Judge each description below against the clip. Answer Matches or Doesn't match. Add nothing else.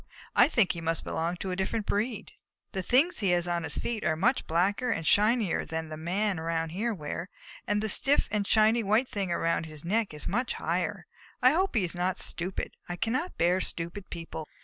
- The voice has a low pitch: Doesn't match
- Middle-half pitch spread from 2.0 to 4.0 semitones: Doesn't match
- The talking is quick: Matches